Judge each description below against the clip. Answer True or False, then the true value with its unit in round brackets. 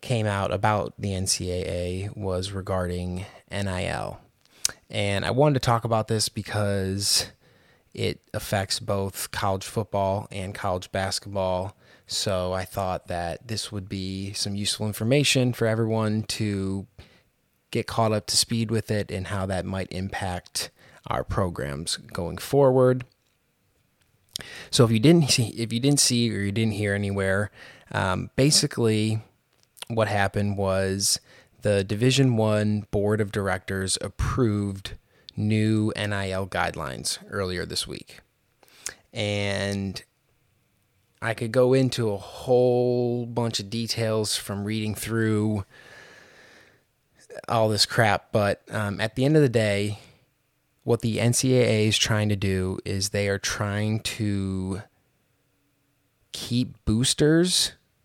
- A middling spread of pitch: True (3.0 semitones)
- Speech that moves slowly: True (125 wpm)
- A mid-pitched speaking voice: False (105 Hz)